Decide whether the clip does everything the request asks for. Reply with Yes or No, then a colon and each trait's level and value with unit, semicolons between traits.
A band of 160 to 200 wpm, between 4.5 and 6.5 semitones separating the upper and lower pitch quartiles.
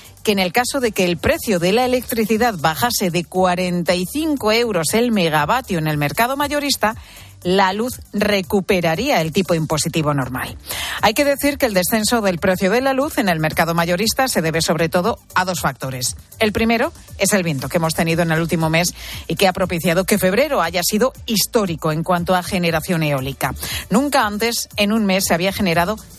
Yes: fast, 190 wpm; average, 5.3 semitones